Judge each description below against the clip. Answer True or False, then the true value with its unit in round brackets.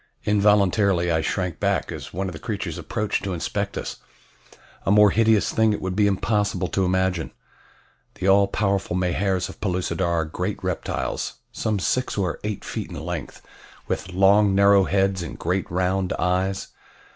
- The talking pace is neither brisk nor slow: True (165 wpm)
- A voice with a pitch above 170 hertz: False (95 Hz)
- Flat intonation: True (2.0 semitones)